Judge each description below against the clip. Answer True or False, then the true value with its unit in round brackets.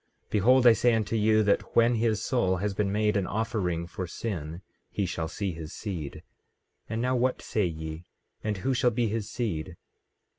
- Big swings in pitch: False (4.3 semitones)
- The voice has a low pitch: True (105 Hz)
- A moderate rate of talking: True (185 wpm)